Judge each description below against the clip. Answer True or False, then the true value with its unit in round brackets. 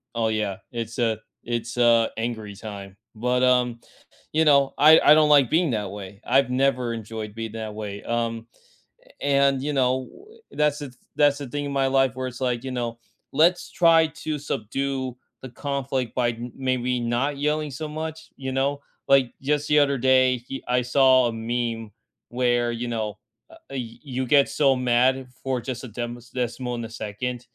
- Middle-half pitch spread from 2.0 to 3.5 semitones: True (2.9 semitones)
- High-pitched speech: False (125 Hz)